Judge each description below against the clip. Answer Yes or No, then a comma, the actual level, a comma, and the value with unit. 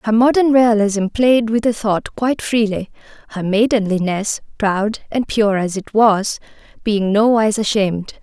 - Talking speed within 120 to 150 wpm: Yes, average, 145 wpm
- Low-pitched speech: No, high, 215 Hz